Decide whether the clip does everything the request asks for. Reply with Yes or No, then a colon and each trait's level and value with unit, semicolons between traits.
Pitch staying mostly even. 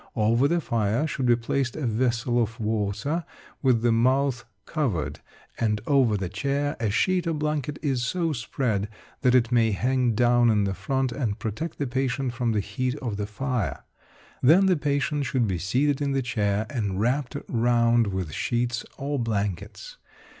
No: average, 4.0 semitones